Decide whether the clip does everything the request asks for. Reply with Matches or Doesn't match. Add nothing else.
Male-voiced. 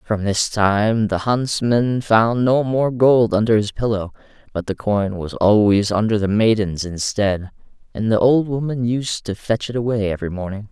Matches